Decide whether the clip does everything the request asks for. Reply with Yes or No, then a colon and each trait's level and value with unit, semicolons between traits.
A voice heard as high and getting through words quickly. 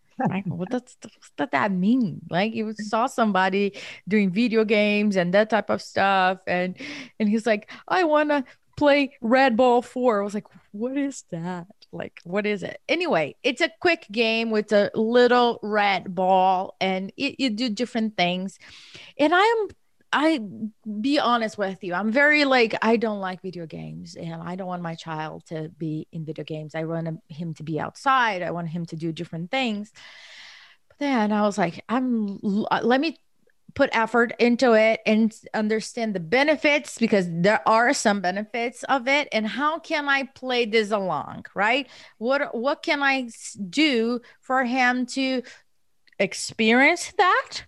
No: high, 220 Hz; average, 170 wpm